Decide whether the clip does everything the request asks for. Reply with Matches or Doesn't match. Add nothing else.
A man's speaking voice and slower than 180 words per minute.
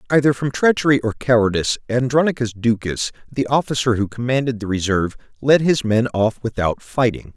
Matches